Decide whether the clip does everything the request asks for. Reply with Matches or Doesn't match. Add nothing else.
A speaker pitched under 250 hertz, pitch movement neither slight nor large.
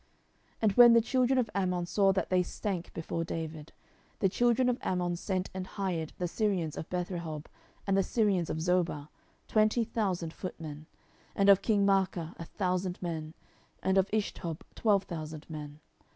Matches